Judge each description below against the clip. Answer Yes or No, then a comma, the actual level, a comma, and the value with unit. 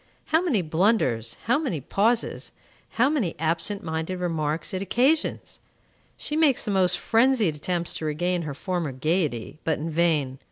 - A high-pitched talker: No, medium, 175 Hz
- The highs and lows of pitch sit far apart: Yes, wide, 6.5 semitones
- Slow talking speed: No, average, 155 wpm